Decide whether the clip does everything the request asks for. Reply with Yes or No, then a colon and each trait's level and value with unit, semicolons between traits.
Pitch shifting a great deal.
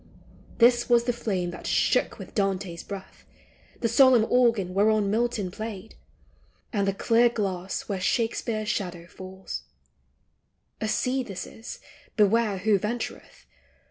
No: average, 3.4 semitones